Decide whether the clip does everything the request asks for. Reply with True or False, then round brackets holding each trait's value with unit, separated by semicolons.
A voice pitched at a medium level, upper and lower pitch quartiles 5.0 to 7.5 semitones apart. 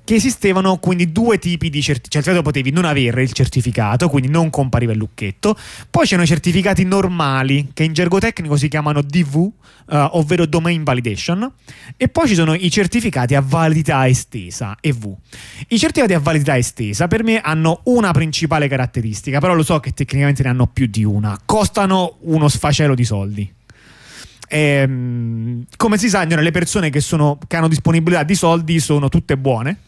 True (155 Hz; 5.3 semitones)